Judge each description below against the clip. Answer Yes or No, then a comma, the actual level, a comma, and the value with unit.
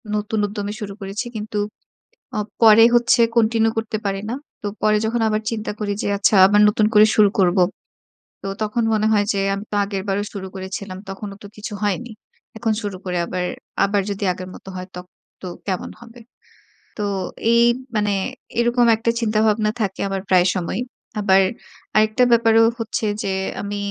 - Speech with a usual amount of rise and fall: No, narrow, 2.0 semitones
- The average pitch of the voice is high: Yes, high, 210 Hz